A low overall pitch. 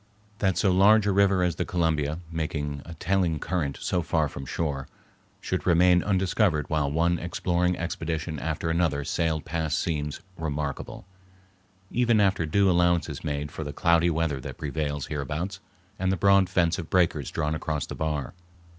Yes: very low, 80 Hz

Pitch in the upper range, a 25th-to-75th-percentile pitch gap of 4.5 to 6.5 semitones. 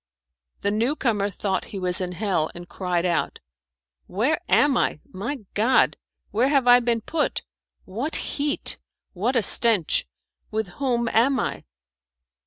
Yes: high, 220 Hz; average, 5.2 semitones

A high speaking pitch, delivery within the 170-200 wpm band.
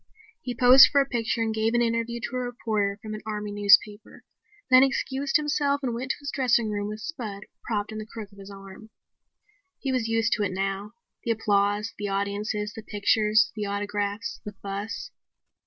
Yes: high, 215 Hz; average, 190 wpm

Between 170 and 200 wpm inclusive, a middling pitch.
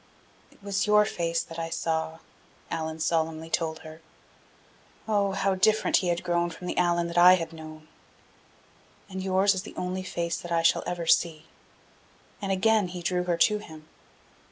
Yes: average, 175 wpm; medium, 175 Hz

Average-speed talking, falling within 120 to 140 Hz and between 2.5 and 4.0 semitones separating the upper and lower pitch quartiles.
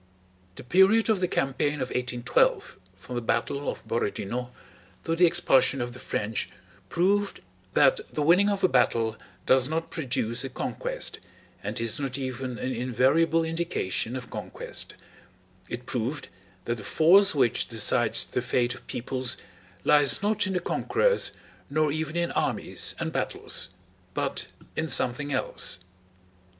No: average, 145 wpm; low, 135 Hz; average, 5.2 semitones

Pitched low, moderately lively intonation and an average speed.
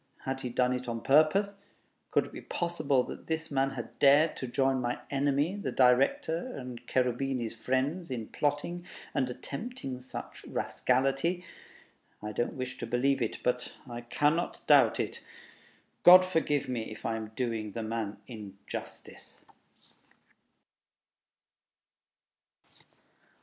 No: low, 130 Hz; average, 3.4 semitones; slow, 130 wpm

